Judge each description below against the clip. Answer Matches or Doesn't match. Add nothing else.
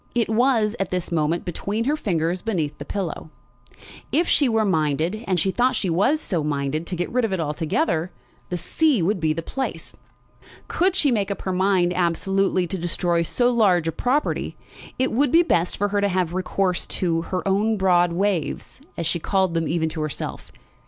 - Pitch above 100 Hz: Matches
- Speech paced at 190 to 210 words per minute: Matches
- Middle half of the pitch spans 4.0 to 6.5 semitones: Matches